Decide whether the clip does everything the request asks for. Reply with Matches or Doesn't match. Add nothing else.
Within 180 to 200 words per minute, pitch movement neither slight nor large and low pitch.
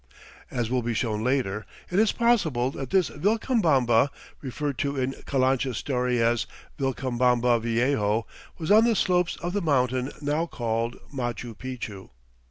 Doesn't match